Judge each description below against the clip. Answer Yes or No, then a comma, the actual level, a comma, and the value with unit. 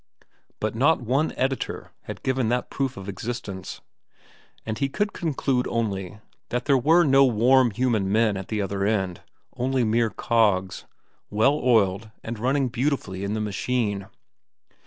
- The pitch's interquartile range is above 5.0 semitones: No, average, 4.4 semitones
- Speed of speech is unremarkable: Yes, average, 150 wpm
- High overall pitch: No, low, 115 Hz